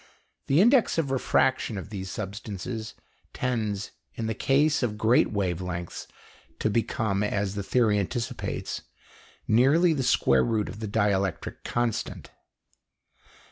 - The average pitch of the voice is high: No, low, 110 Hz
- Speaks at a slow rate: Yes, slow, 130 wpm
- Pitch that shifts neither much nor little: Yes, average, 3.9 semitones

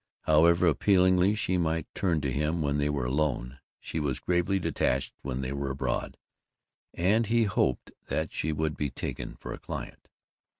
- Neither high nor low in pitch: No, very low, 80 Hz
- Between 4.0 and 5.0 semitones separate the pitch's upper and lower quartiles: Yes, average, 4.4 semitones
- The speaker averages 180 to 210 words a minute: No, average, 170 wpm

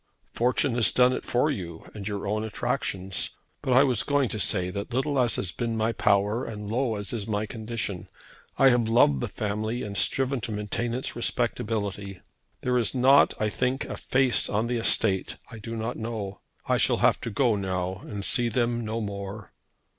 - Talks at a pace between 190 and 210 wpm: Yes, average, 195 wpm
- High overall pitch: No, low, 110 Hz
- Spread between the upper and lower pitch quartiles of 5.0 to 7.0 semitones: No, average, 3.3 semitones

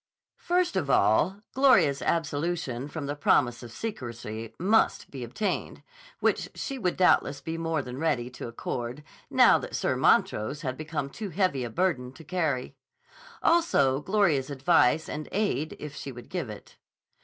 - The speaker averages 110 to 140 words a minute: No, average, 155 wpm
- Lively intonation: Yes, wide, 5.9 semitones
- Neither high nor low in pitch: Yes, medium, 150 Hz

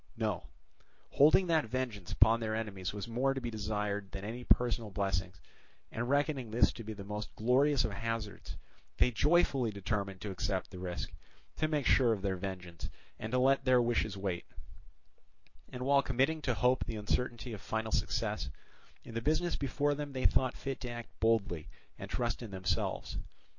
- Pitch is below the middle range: Yes, low, 115 Hz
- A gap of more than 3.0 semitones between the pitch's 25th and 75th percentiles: Yes, average, 4.2 semitones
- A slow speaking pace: No, average, 180 wpm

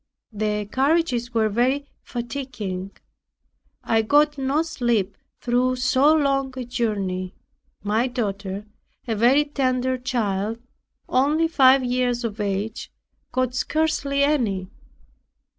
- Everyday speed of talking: No, slow, 110 wpm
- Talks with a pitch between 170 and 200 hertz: No, high, 245 Hz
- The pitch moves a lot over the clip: No, average, 4.3 semitones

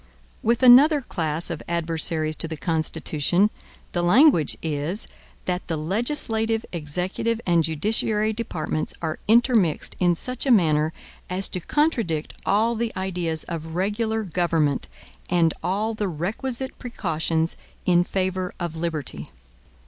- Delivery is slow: Yes, slow, 125 wpm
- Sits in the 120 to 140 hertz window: No, medium, 180 Hz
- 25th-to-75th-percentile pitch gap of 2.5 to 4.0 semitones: No, wide, 5.4 semitones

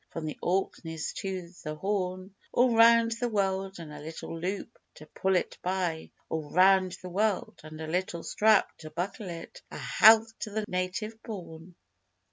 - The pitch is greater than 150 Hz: Yes, medium, 185 Hz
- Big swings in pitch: No, average, 4.1 semitones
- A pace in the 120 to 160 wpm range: No, average, 170 wpm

